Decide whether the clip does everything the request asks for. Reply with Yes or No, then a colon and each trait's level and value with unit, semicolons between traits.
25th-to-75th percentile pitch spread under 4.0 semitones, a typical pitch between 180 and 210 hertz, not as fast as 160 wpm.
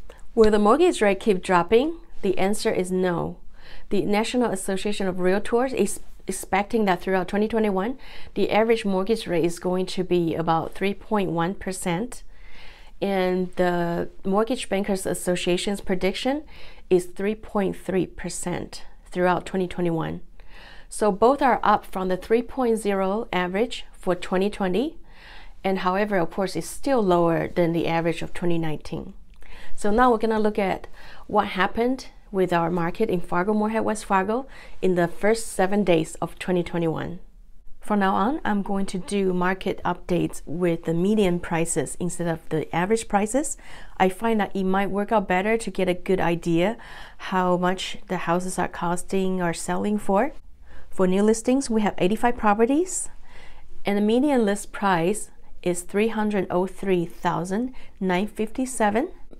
Yes: average, 3.2 semitones; high, 190 Hz; average, 140 wpm